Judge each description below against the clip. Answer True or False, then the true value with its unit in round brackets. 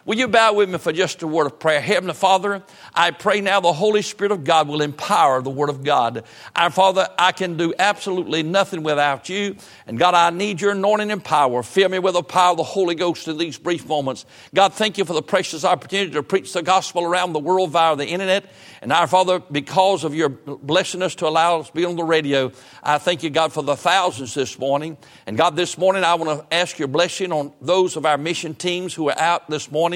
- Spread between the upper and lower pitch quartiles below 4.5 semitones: True (3.7 semitones)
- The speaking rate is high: True (240 wpm)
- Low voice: False (175 Hz)